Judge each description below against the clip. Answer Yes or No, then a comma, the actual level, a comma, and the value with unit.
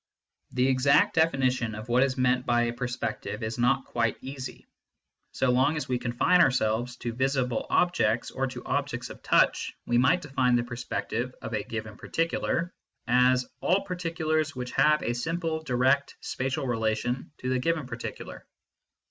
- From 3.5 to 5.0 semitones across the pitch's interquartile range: No, average, 2.8 semitones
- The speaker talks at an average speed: Yes, average, 165 wpm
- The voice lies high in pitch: No, low, 125 Hz